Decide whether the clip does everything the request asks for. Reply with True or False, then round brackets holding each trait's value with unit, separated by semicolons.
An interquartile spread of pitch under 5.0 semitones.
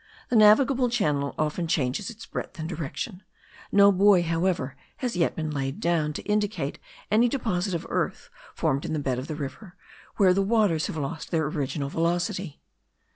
False (5.4 semitones)